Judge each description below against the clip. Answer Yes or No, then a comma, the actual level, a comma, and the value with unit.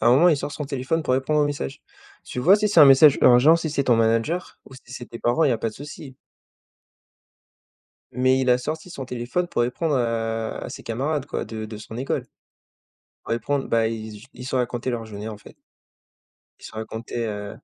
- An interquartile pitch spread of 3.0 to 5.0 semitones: Yes, average, 4.1 semitones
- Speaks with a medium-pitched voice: No, low, 125 Hz